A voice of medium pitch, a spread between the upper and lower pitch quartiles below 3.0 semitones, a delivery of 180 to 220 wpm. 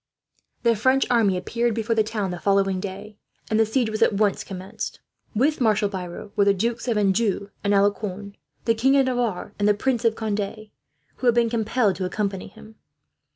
No: high, 215 Hz; narrow, 2.6 semitones; average, 200 wpm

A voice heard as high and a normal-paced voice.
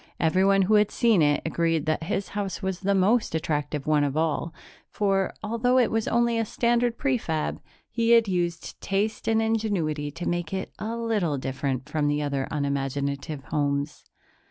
No: medium, 175 Hz; average, 170 wpm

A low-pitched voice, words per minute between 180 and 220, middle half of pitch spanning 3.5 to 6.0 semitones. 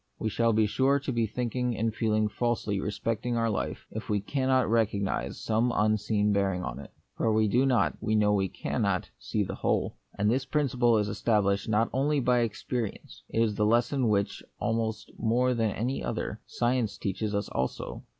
No: low, 110 Hz; average, 185 wpm; average, 2.7 semitones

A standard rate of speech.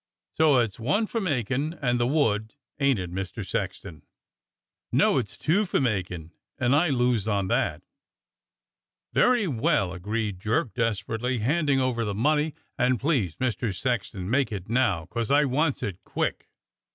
Yes: average, 150 wpm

